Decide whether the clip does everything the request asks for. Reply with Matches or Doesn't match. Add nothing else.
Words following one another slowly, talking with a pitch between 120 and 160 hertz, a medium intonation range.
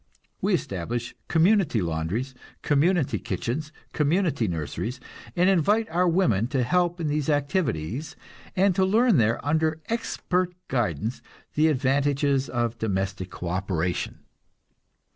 Doesn't match